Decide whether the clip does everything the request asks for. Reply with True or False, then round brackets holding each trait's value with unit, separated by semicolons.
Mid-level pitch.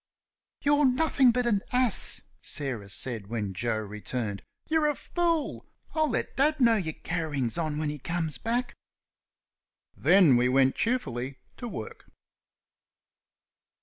True (165 Hz)